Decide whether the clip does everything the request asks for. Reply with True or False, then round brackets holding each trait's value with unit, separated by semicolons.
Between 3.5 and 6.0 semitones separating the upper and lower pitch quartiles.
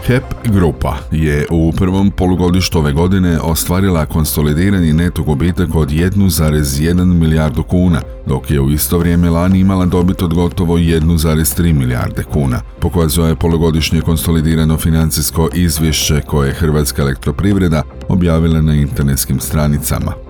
False (2.5 semitones)